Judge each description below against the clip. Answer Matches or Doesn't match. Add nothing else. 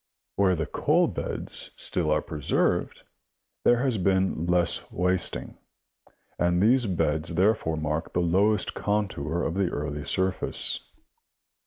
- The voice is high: Doesn't match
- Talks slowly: Matches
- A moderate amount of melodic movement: Matches